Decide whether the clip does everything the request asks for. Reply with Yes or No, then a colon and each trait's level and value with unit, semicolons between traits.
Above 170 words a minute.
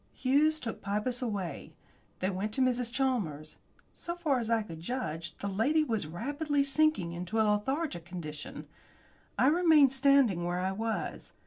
No: average, 155 wpm